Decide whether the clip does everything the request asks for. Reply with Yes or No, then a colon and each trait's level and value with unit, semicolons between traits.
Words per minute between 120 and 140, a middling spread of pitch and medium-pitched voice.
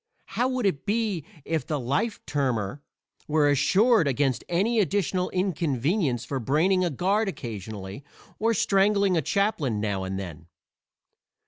No: slow, 135 wpm; wide, 7.8 semitones; medium, 160 Hz